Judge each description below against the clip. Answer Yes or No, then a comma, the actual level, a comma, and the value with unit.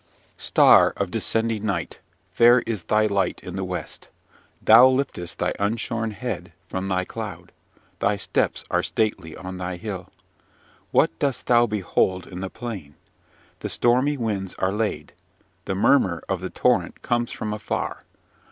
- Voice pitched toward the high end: No, low, 105 Hz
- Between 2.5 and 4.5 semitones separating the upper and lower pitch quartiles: Yes, average, 3.8 semitones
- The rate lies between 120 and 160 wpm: Yes, average, 150 wpm